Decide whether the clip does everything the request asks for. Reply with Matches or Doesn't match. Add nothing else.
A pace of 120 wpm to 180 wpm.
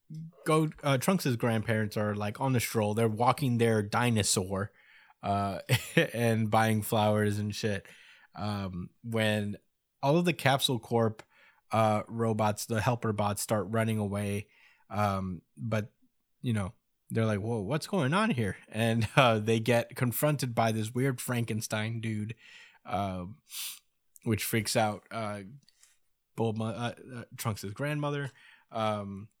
Matches